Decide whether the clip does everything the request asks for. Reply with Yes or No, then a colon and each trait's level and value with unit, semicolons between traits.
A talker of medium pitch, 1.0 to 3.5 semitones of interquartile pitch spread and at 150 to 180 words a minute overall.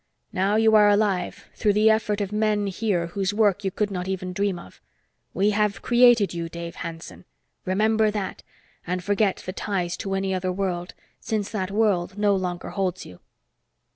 No: high, 195 Hz; narrow, 2.5 semitones; average, 175 wpm